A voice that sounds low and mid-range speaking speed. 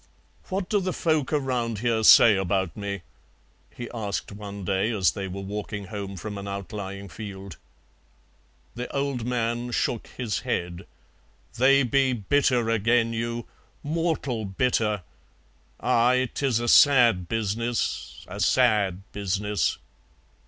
No: low, 110 Hz; slow, 125 wpm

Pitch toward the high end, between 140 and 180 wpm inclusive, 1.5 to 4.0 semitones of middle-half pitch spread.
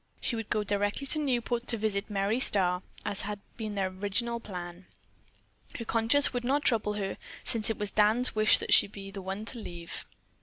No: high, 210 Hz; average, 195 wpm; average, 3.0 semitones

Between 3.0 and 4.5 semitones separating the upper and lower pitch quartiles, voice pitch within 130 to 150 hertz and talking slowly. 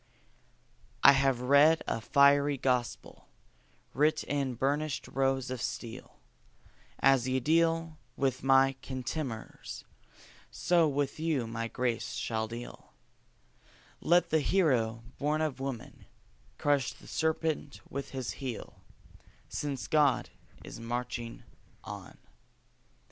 Yes: average, 3.3 semitones; low, 135 Hz; slow, 110 wpm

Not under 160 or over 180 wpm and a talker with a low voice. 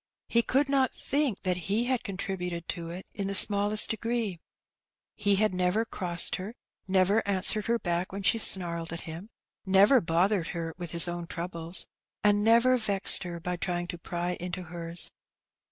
No: average, 170 wpm; medium, 185 Hz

